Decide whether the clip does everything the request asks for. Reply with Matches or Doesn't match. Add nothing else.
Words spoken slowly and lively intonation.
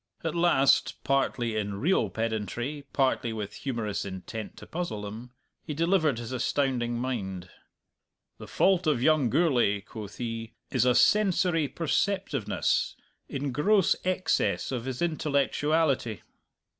Matches